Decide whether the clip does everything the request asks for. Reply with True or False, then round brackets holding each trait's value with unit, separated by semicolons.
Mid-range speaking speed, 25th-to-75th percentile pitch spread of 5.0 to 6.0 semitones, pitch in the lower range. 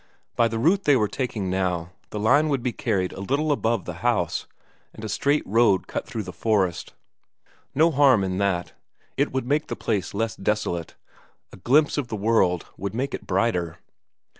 True (190 wpm; 5.6 semitones; 110 Hz)